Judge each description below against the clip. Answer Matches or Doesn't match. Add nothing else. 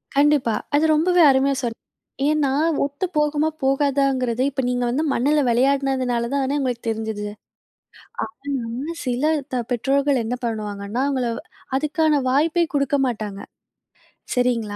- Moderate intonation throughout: Matches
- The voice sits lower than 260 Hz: Doesn't match